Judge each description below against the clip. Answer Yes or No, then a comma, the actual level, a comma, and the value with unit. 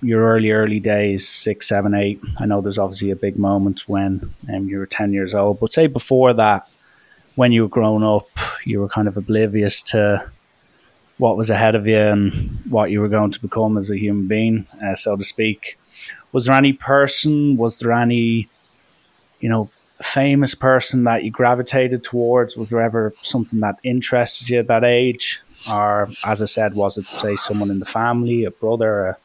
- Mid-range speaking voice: No, low, 110 Hz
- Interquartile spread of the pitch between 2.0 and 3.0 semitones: Yes, average, 2.7 semitones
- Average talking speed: Yes, average, 195 wpm